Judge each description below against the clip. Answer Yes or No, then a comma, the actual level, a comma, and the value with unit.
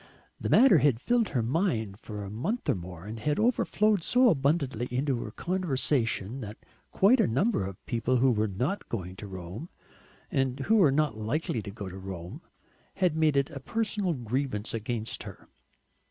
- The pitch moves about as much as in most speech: No, wide, 7.6 semitones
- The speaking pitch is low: Yes, low, 130 Hz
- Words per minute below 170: No, average, 180 wpm